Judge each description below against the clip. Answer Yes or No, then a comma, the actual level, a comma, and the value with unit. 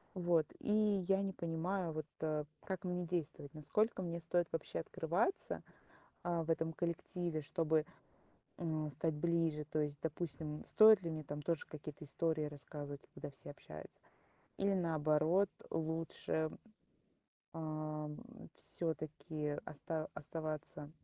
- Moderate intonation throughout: No, narrow, 2.2 semitones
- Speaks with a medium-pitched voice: Yes, medium, 160 Hz